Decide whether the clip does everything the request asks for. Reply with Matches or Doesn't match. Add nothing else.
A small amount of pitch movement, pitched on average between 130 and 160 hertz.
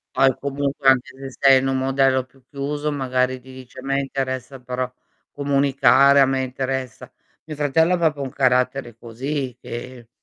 Matches